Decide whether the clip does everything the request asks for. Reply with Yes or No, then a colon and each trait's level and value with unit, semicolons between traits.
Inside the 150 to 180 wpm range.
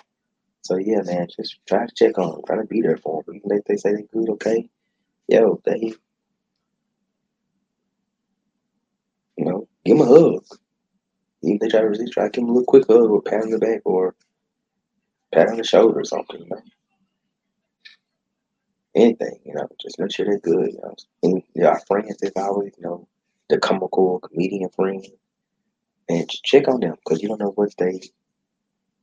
No: average, 190 wpm